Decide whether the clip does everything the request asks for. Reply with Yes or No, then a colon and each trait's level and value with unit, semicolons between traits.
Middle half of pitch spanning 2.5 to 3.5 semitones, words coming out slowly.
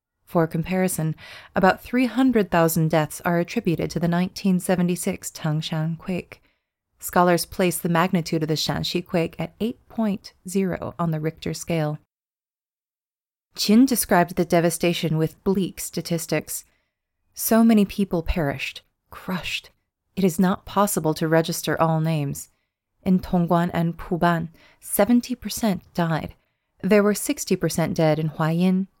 Yes: average, 3.0 semitones; slow, 130 wpm